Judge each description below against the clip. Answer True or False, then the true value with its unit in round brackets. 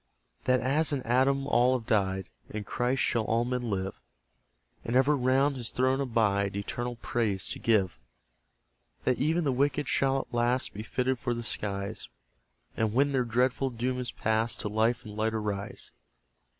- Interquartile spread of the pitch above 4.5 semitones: False (3.1 semitones)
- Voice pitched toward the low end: True (120 Hz)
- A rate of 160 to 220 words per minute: True (170 wpm)